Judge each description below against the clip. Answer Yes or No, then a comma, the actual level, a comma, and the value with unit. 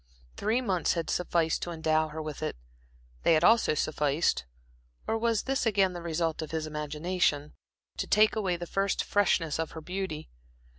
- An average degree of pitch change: Yes, average, 4.0 semitones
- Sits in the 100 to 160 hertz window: No, medium, 170 Hz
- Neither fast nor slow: Yes, average, 170 wpm